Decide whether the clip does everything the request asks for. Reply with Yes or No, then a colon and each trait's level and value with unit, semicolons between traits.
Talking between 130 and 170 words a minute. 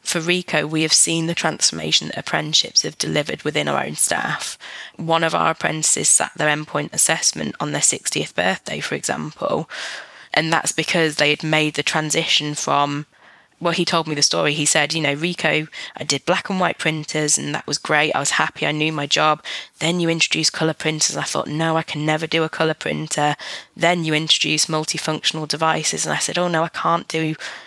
No: fast, 205 wpm